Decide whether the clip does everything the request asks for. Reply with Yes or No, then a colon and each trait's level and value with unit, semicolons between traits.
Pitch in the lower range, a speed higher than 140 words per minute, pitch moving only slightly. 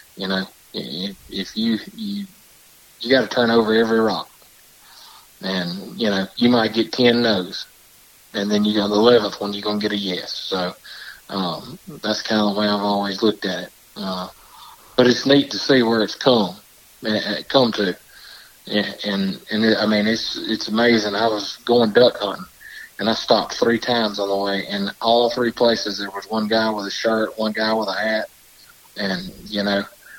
Yes: low, 110 Hz; average, 195 wpm; narrow, 2.3 semitones